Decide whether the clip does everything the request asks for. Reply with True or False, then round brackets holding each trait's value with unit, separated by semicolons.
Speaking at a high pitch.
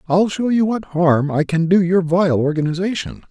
False (175 Hz)